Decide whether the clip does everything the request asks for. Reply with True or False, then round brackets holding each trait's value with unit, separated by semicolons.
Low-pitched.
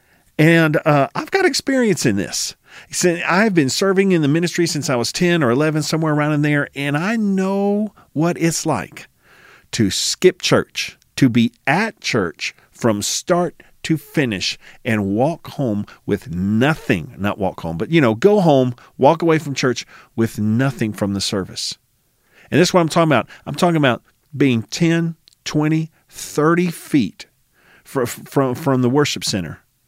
False (150 Hz)